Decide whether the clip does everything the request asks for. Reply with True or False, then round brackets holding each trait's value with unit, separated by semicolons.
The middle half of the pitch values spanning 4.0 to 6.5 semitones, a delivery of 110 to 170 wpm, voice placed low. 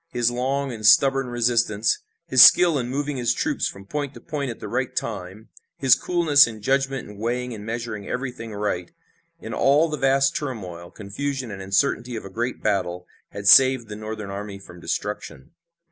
False (4.6 semitones; 180 wpm; 120 Hz)